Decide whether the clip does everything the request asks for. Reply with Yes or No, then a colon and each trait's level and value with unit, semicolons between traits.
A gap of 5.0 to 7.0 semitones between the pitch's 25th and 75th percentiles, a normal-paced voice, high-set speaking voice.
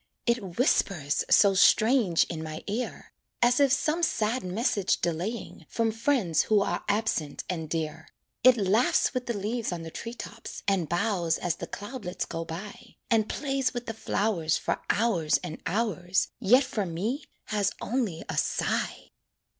Yes: wide, 5.5 semitones; average, 160 wpm; high, 205 Hz